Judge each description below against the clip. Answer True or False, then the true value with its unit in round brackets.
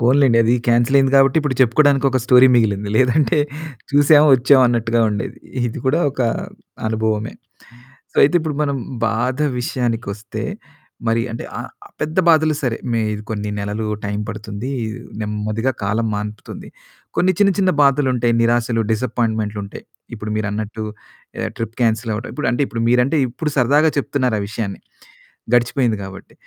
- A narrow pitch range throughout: False (3.9 semitones)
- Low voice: True (120 Hz)